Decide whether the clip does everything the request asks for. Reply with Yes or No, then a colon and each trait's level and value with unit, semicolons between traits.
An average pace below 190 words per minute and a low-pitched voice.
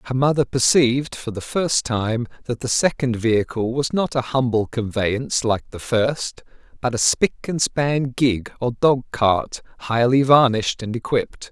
Yes: average, 165 wpm; low, 125 Hz